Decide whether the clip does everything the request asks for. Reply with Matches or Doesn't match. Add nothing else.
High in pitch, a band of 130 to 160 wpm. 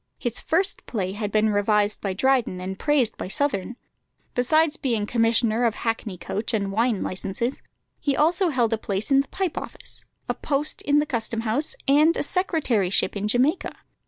Doesn't match